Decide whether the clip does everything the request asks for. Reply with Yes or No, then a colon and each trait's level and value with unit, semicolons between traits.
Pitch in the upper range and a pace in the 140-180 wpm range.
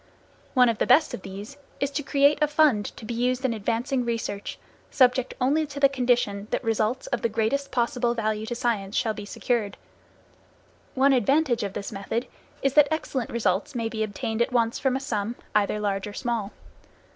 No: high, 235 Hz; average, 190 wpm